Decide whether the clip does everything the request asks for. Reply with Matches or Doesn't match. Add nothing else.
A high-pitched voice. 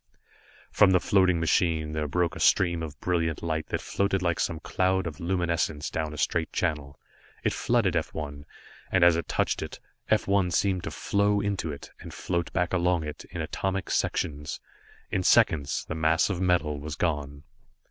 Doesn't match